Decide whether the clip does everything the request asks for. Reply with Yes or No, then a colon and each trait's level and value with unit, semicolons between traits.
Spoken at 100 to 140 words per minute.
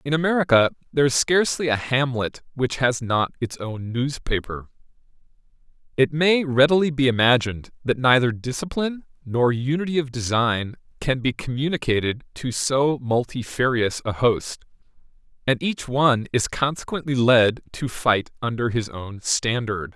Yes: slow, 135 wpm